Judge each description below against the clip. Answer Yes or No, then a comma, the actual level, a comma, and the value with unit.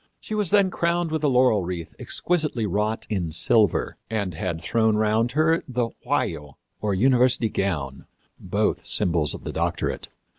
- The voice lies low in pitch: Yes, low, 110 Hz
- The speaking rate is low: No, average, 155 wpm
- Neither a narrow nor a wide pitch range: No, wide, 6.7 semitones